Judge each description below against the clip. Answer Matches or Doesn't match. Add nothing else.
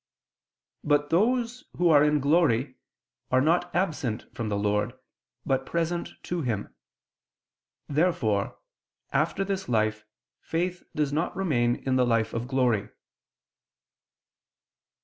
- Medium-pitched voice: Matches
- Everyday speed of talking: Doesn't match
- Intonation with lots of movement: Matches